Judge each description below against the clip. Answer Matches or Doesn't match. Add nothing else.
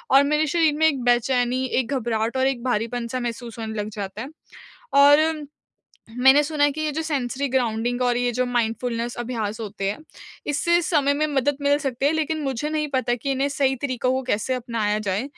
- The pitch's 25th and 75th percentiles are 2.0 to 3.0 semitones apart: Doesn't match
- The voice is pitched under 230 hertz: Doesn't match